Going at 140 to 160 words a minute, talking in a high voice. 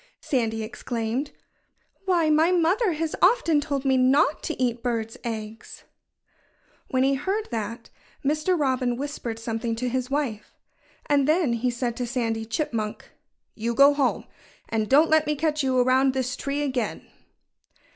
Yes: average, 150 wpm; very high, 260 Hz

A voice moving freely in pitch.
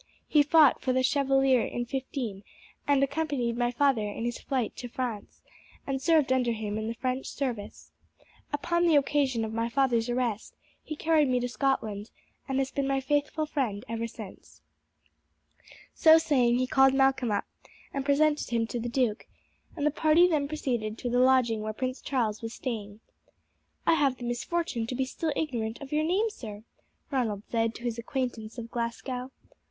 No: average, 3.5 semitones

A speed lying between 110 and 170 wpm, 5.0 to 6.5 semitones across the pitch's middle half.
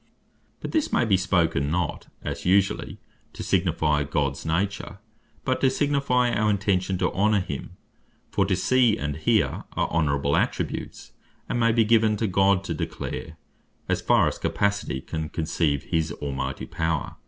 Yes: average, 160 wpm; average, 5.3 semitones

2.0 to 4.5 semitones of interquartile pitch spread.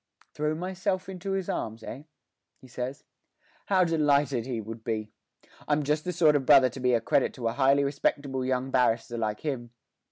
Yes: average, 4.0 semitones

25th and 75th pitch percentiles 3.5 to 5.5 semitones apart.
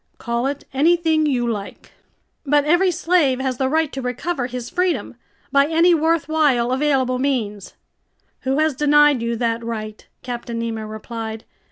Yes: average, 4.7 semitones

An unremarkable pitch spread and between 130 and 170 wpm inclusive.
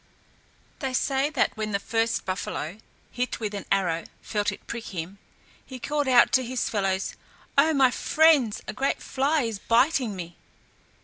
Yes: average, 5.0 semitones; average, 165 wpm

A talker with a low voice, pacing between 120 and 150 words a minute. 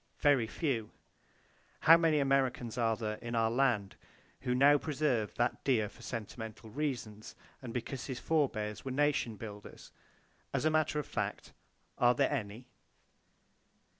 Yes: low, 125 Hz; average, 140 wpm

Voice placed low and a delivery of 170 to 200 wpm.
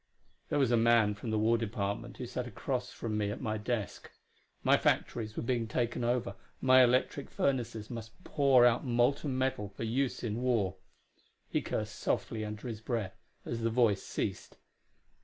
Yes: low, 115 Hz; average, 175 wpm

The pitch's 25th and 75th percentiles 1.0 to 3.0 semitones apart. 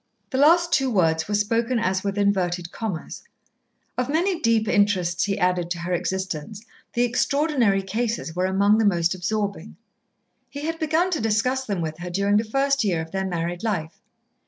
No: average, 5.2 semitones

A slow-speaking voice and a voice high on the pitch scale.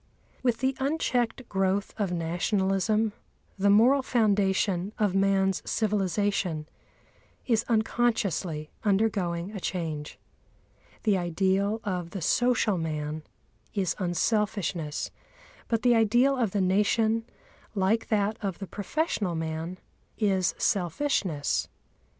Yes: slow, 105 wpm; high, 200 Hz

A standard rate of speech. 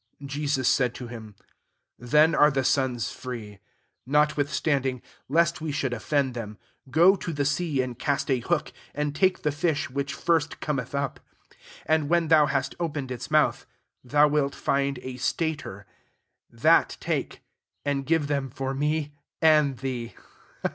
Yes: average, 160 wpm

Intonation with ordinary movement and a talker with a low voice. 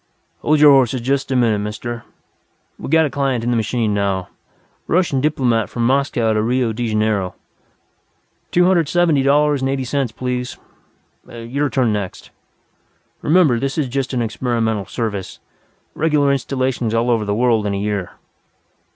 Yes: average, 3.8 semitones; low, 125 Hz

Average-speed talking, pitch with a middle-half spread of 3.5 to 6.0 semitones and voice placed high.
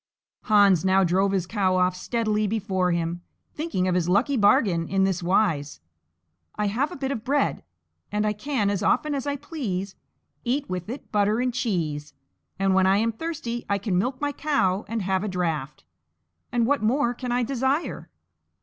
Yes: average, 185 wpm; average, 5.0 semitones; high, 205 Hz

